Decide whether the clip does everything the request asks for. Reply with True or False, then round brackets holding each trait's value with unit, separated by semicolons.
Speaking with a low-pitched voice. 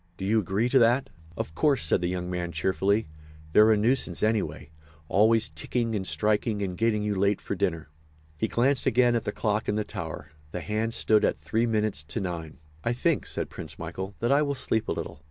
True (105 Hz)